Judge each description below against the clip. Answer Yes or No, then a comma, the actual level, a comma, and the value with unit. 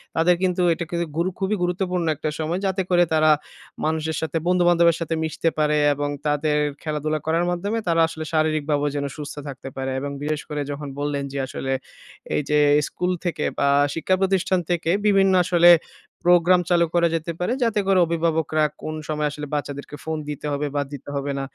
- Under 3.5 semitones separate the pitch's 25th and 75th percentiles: Yes, average, 2.9 semitones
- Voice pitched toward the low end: No, medium, 160 Hz